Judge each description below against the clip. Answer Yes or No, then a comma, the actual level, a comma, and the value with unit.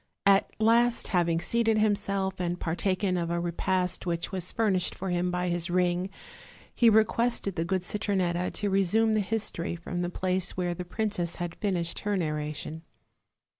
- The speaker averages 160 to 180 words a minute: Yes, average, 165 wpm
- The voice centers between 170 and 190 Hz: Yes, medium, 185 Hz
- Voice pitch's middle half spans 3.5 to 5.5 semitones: No, average, 2.9 semitones